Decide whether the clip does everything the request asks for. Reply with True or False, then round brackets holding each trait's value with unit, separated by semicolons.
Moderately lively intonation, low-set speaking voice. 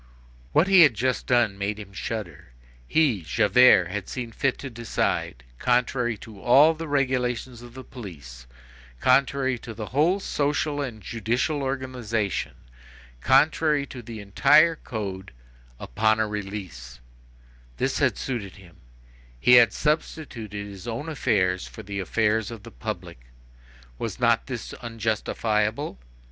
True (4.5 semitones; 115 Hz)